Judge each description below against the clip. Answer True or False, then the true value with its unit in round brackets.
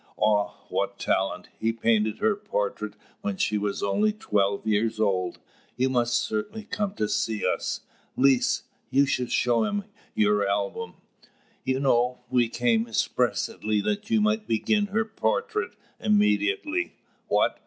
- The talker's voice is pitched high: False (120 Hz)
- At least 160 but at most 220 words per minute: False (140 wpm)